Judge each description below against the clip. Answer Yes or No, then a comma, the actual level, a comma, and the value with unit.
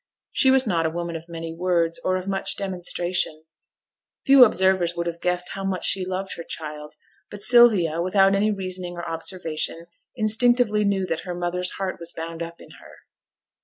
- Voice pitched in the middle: Yes, medium, 180 Hz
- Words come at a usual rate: Yes, average, 180 wpm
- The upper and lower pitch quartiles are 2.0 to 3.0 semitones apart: Yes, narrow, 2.6 semitones